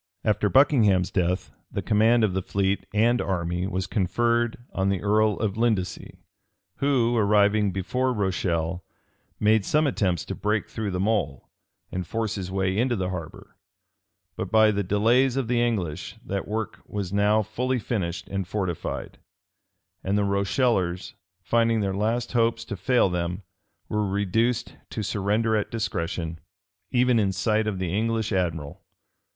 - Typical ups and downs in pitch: Yes, average, 3.4 semitones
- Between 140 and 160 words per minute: Yes, average, 150 wpm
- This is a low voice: Yes, low, 105 Hz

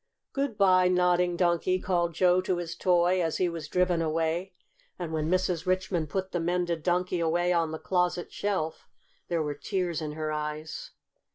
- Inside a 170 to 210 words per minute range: Yes, average, 175 wpm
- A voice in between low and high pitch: Yes, medium, 175 Hz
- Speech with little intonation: Yes, narrow, 2.0 semitones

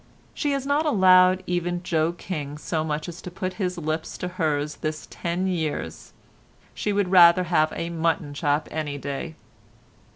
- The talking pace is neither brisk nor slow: Yes, average, 165 wpm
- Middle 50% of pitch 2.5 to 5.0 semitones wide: Yes, average, 2.8 semitones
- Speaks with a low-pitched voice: No, medium, 170 Hz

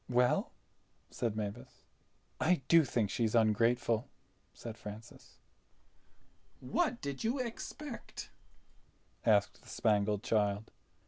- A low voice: Yes, low, 115 Hz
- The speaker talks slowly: Yes, slow, 95 wpm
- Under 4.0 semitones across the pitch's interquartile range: No, average, 5.0 semitones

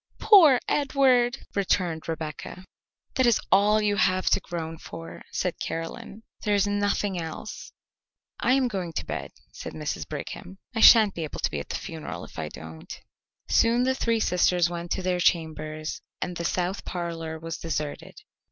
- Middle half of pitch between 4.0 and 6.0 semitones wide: Yes, average, 4.6 semitones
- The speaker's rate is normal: Yes, average, 170 wpm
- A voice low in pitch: No, medium, 180 Hz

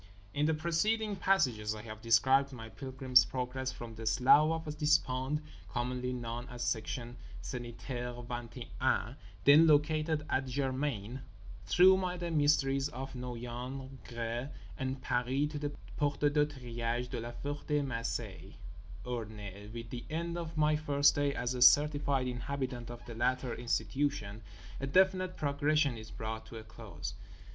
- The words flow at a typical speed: Yes, average, 150 wpm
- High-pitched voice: No, low, 130 Hz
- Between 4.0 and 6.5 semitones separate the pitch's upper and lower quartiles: No, average, 3.6 semitones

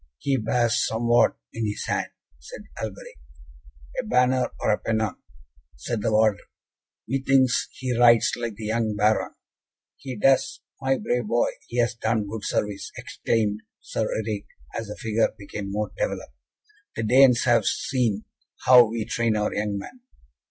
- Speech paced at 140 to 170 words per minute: Yes, average, 150 wpm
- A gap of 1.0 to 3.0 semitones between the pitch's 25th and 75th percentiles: Yes, narrow, 2.4 semitones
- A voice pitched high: No, low, 115 Hz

